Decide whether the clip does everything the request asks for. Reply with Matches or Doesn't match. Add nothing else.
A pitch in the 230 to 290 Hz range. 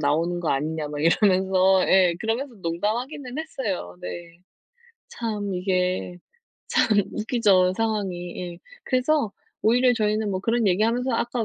Doesn't match